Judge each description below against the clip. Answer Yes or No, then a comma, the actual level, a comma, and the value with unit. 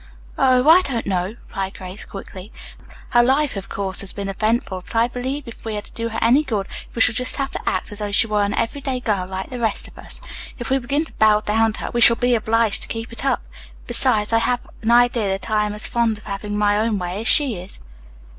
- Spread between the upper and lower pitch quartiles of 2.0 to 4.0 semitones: Yes, average, 3.2 semitones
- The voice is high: Yes, high, 225 Hz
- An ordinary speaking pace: No, fast, 250 wpm